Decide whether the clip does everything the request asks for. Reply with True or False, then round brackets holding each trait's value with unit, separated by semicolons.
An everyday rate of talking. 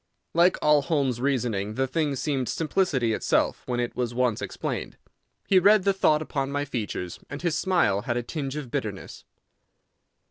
True (170 wpm)